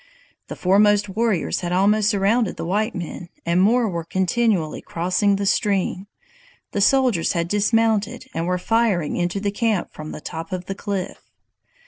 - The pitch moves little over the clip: No, average, 3.2 semitones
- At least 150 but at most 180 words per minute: Yes, average, 160 wpm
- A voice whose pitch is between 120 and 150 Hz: No, high, 195 Hz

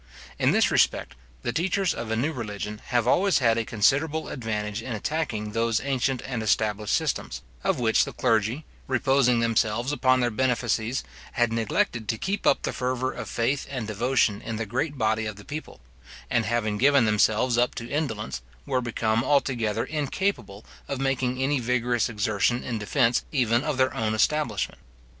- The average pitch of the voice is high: No, low, 120 Hz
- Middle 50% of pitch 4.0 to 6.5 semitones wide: No, average, 3.3 semitones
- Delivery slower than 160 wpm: No, average, 170 wpm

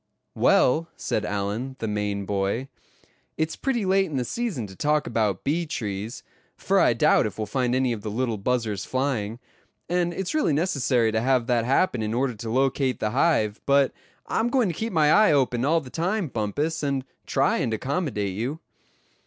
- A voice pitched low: Yes, low, 130 Hz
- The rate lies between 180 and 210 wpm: Yes, average, 185 wpm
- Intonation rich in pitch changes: Yes, wide, 6.2 semitones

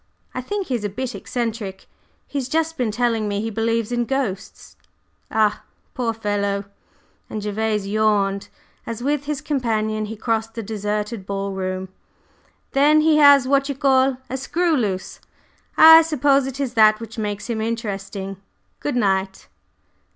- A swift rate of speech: No, average, 155 wpm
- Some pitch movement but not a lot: Yes, average, 4.5 semitones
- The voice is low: No, high, 225 Hz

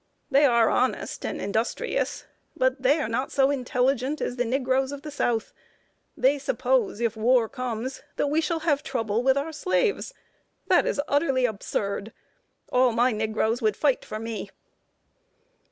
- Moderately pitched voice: No, very high, 255 Hz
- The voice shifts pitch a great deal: No, average, 3.7 semitones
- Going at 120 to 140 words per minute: No, average, 160 wpm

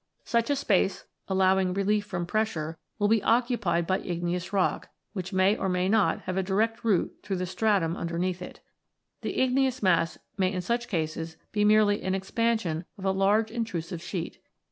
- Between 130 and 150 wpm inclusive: No, average, 180 wpm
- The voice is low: No, high, 190 Hz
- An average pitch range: Yes, average, 3.3 semitones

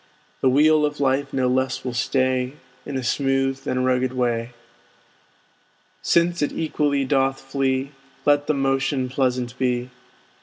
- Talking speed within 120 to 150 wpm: Yes, average, 140 wpm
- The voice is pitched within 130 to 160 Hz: Yes, low, 135 Hz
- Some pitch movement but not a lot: No, narrow, 1.7 semitones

